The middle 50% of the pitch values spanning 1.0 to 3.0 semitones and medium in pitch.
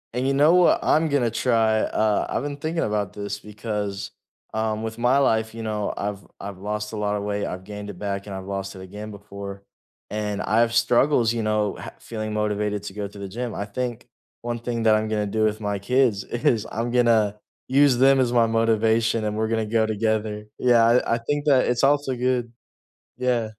No: narrow, 2.5 semitones; low, 110 Hz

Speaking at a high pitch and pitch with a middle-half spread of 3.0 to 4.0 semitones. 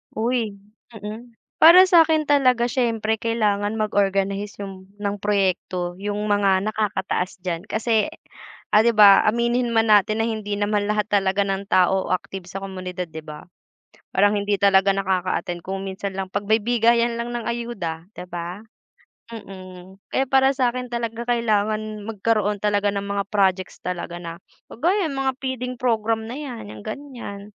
Yes: high, 210 Hz; average, 3.4 semitones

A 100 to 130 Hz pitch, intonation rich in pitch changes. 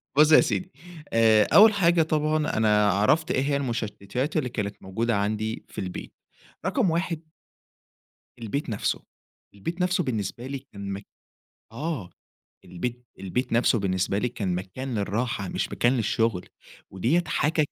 Yes: low, 120 Hz; wide, 7.0 semitones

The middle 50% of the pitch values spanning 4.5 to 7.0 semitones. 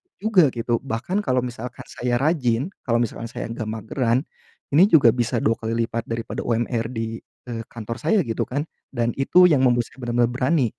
No: average, 2.8 semitones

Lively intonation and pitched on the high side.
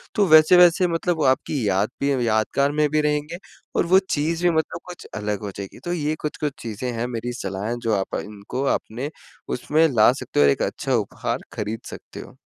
No: wide, 6.5 semitones; medium, 140 Hz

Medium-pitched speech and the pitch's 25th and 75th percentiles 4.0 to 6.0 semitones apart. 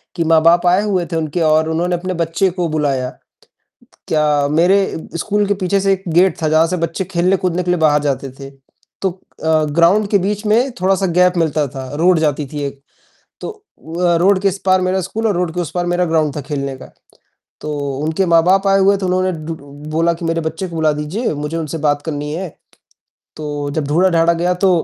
No: medium, 170 Hz; average, 3.3 semitones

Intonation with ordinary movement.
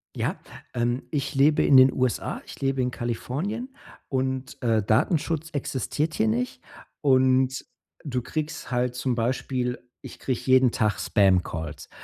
No: narrow, 2.3 semitones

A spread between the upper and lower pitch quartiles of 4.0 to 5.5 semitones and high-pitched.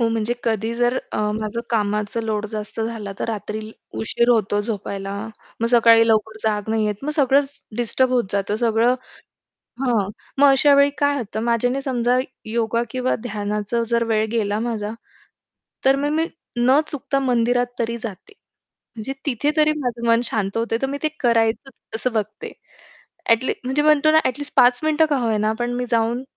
No: average, 3.0 semitones; high, 235 Hz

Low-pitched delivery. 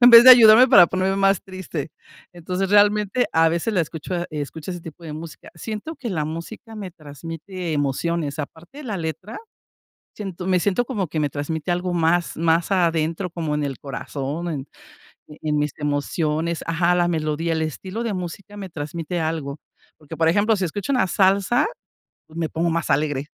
No: medium, 170 Hz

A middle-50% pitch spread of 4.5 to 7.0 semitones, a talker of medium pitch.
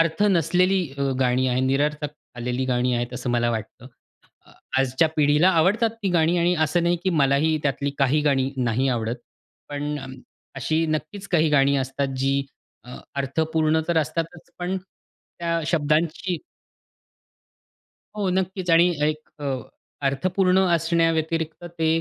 No: average, 3.9 semitones; medium, 155 Hz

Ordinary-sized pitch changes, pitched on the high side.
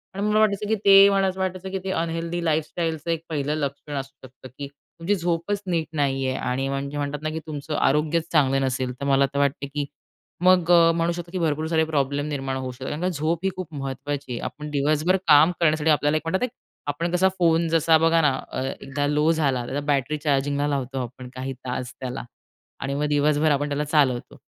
No: average, 3.2 semitones; medium, 150 Hz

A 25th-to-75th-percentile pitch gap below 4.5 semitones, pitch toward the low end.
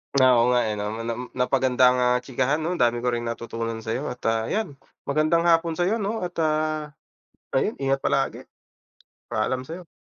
No: average, 4.9 semitones; low, 130 Hz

